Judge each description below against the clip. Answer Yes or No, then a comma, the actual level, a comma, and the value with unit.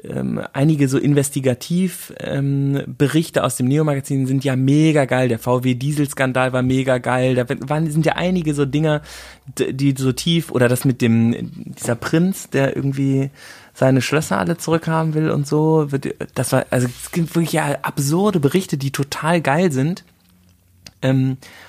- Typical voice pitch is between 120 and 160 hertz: Yes, medium, 140 Hz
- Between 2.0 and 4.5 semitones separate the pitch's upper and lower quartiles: Yes, average, 3.4 semitones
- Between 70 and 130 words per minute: No, average, 155 wpm